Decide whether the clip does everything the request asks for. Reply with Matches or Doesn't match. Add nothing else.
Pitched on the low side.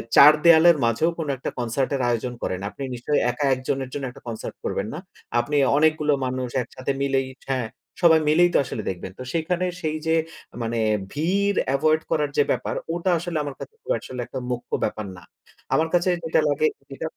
Doesn't match